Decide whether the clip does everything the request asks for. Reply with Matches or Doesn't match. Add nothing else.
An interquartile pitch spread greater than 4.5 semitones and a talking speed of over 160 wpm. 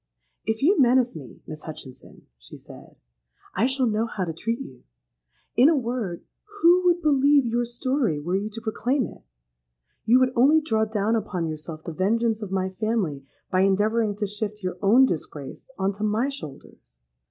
Matches